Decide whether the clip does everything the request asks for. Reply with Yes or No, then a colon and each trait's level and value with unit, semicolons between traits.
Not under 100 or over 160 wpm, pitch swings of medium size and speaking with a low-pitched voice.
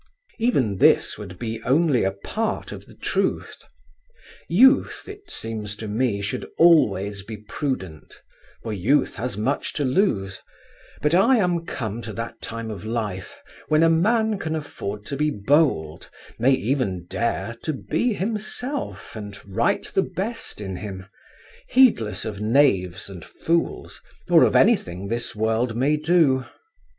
No: average, 145 wpm; wide, 7.9 semitones; low, 120 Hz